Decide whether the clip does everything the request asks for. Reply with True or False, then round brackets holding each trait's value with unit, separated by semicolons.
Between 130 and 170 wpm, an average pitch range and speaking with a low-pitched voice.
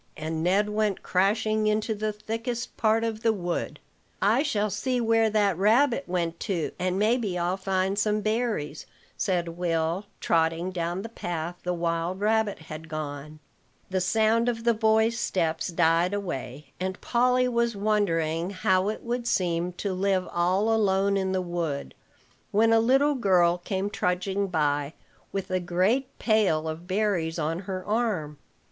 False (155 wpm; 4.1 semitones; 190 Hz)